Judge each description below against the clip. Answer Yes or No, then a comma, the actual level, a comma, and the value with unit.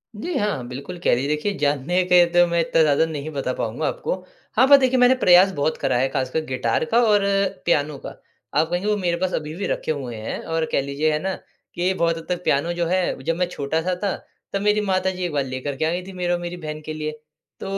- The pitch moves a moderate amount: Yes, average, 4.2 semitones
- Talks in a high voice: No, medium, 165 Hz